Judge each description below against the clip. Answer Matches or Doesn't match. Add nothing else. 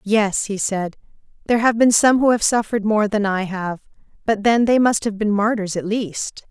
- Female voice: Matches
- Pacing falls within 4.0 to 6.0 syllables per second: Matches